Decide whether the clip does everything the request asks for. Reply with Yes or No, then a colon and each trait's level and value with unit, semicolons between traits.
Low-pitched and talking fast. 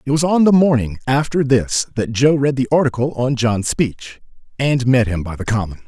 Yes: low, 125 Hz; fast, 215 wpm